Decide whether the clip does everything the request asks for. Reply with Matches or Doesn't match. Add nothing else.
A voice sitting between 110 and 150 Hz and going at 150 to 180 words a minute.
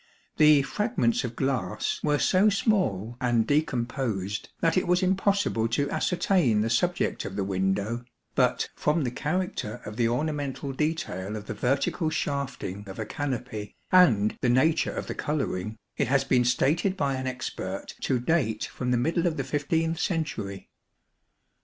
Matches